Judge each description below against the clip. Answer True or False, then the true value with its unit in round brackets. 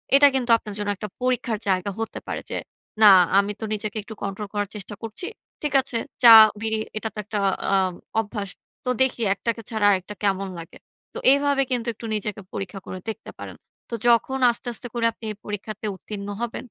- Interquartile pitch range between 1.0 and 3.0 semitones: True (2.6 semitones)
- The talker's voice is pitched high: True (215 Hz)